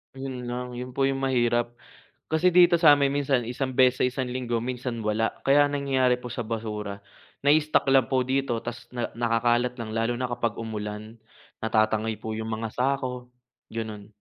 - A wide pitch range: No, average, 2.9 semitones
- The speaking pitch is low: Yes, low, 125 Hz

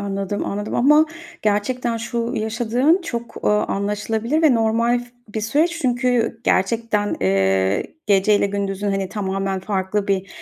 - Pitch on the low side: No, high, 210 Hz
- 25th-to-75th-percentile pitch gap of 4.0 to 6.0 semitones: No, average, 3.3 semitones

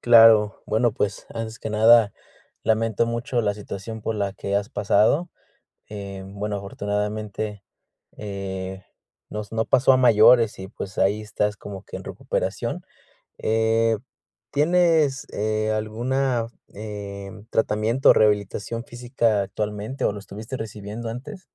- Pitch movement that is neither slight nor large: No, narrow, 2.2 semitones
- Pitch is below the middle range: Yes, low, 110 Hz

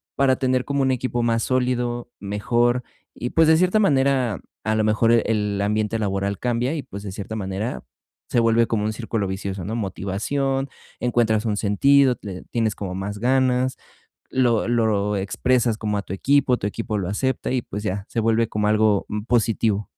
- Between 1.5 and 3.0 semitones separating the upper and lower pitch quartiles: No, average, 3.5 semitones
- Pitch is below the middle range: Yes, low, 115 Hz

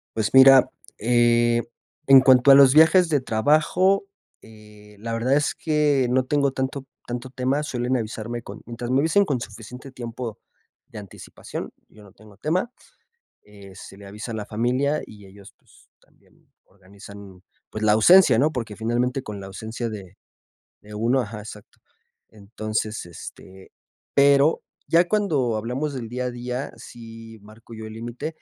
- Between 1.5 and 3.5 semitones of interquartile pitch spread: No, average, 4.0 semitones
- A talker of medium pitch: No, low, 120 Hz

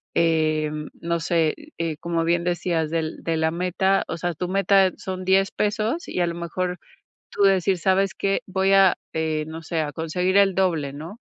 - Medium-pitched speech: Yes, medium, 175 Hz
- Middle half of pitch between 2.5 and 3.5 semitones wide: Yes, average, 2.8 semitones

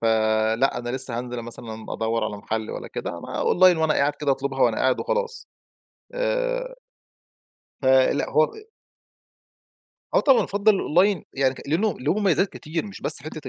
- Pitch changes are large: Yes, wide, 8.4 semitones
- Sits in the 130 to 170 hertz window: Yes, medium, 140 Hz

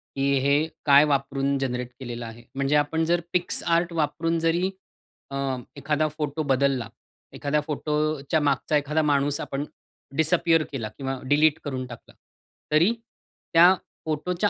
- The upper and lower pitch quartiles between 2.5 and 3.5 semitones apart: Yes, average, 2.8 semitones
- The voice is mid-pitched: Yes, medium, 150 Hz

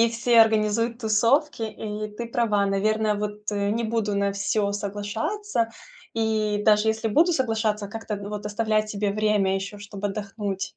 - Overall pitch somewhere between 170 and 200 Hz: No, high, 215 Hz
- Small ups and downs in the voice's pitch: Yes, narrow, 1.7 semitones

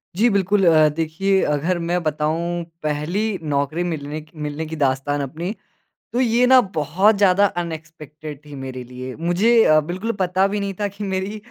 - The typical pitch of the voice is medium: Yes, medium, 165 Hz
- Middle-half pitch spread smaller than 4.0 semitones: No, average, 4.4 semitones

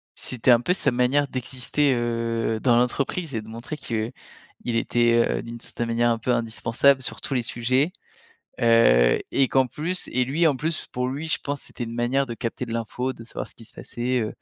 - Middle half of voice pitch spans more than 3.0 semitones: No, narrow, 2.6 semitones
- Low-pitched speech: Yes, low, 120 Hz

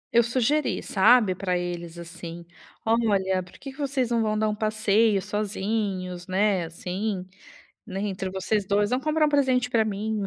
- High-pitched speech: Yes, high, 210 Hz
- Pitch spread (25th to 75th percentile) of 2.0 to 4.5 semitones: Yes, average, 3.6 semitones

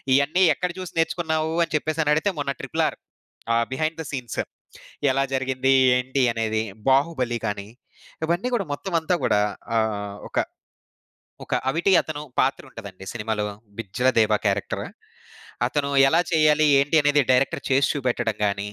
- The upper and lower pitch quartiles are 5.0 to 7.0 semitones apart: Yes, wide, 5.6 semitones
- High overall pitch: No, low, 135 Hz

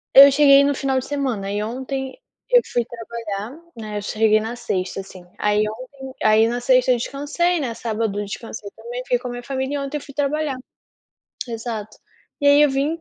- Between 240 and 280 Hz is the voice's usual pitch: Yes, high, 245 Hz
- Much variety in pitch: No, average, 4.2 semitones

